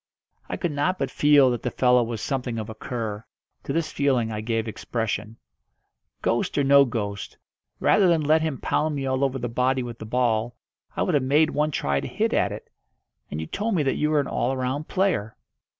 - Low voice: Yes, low, 130 Hz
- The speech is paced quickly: Yes, fast, 215 wpm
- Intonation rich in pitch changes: No, average, 4.5 semitones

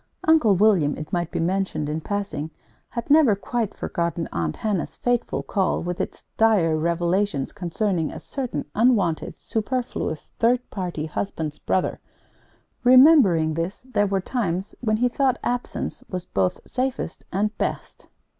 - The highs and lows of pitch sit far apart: Yes, wide, 6.0 semitones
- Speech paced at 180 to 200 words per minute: No, average, 140 wpm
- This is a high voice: Yes, high, 195 Hz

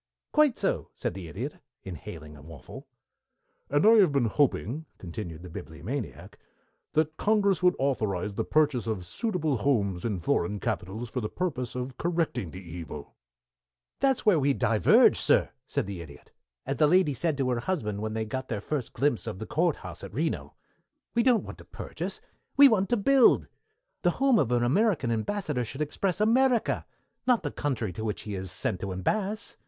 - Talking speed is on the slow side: No, average, 180 wpm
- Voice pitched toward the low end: Yes, low, 130 Hz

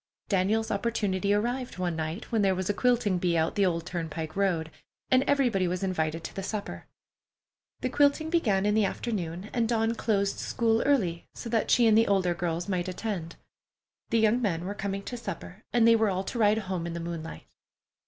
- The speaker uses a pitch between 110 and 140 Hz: No, high, 200 Hz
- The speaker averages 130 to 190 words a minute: No, average, 200 wpm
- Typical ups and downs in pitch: Yes, average, 4.3 semitones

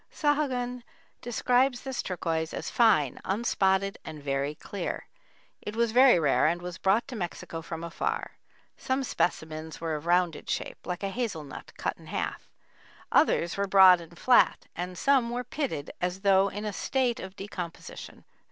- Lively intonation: Yes, wide, 6.3 semitones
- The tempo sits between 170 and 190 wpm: No, average, 160 wpm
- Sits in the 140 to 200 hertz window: Yes, high, 190 Hz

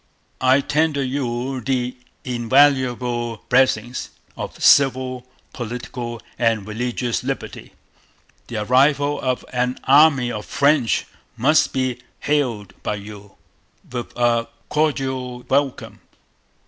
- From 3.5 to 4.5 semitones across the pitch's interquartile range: No, narrow, 2.4 semitones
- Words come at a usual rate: No, slow, 100 wpm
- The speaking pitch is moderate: No, low, 125 Hz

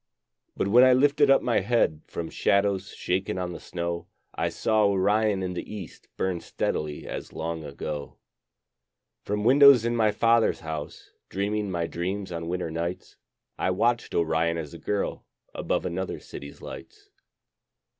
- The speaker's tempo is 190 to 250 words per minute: No, average, 155 wpm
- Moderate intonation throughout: Yes, average, 4.4 semitones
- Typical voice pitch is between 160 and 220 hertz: No, very low, 95 Hz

